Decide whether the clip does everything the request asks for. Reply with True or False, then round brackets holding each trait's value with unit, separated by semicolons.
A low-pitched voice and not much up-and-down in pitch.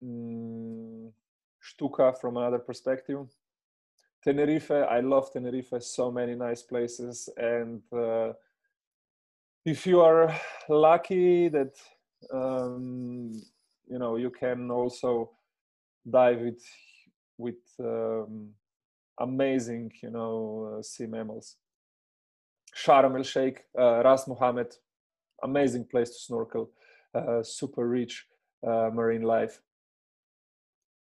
True (120 Hz; 2.3 semitones)